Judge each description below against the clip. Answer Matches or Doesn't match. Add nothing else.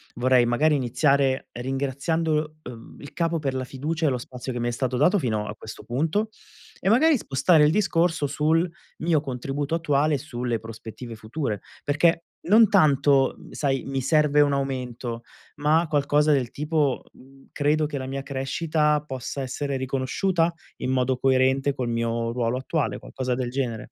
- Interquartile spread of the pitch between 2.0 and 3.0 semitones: Doesn't match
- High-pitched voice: Doesn't match